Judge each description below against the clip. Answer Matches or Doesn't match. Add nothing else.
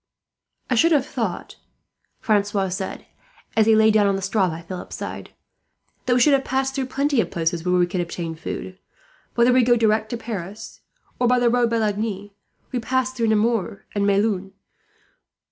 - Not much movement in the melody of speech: Doesn't match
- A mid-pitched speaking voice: Doesn't match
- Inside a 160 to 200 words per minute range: Matches